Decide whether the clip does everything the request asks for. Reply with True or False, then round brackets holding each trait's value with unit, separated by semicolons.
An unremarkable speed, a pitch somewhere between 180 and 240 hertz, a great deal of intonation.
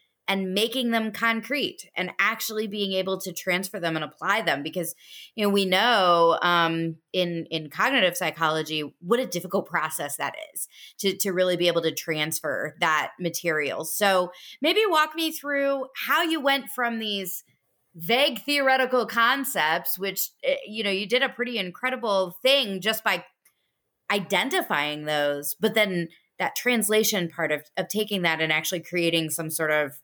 True (160 wpm; 190 Hz; 5.8 semitones)